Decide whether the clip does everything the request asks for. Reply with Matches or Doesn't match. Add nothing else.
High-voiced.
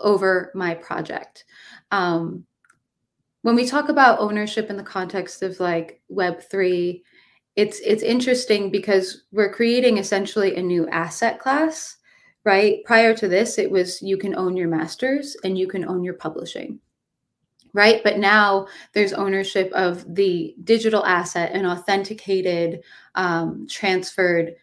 Matches